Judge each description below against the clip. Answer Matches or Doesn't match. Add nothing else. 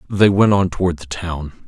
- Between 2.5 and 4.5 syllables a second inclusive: Doesn't match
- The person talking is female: Doesn't match